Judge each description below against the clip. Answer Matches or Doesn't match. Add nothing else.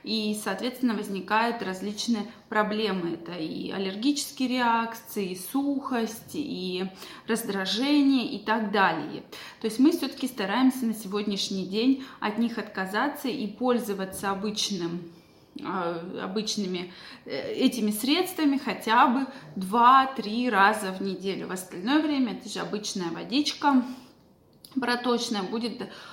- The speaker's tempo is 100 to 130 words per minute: Matches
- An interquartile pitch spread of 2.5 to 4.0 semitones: Doesn't match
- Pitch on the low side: Doesn't match